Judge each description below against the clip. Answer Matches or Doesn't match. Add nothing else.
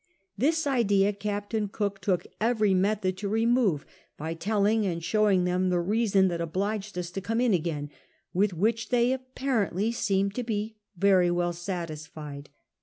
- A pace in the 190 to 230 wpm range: Doesn't match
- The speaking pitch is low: Doesn't match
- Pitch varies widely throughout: Doesn't match